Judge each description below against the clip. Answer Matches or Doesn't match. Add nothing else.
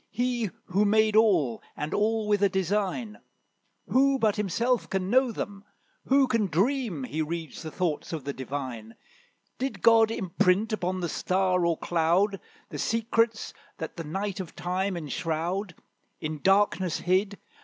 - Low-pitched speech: Doesn't match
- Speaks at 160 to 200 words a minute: Doesn't match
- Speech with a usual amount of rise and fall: Matches